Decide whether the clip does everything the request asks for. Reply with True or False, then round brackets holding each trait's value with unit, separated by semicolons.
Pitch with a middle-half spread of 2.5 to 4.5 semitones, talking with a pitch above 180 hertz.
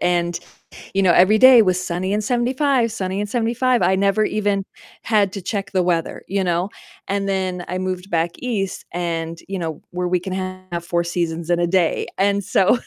True (2.8 semitones; 190 Hz)